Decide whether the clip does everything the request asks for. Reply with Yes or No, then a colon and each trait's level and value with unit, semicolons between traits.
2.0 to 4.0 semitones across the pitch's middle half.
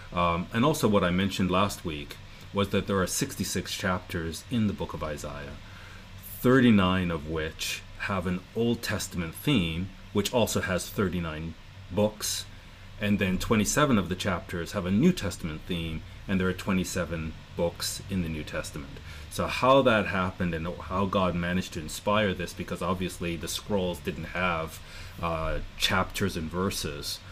Yes: average, 2.7 semitones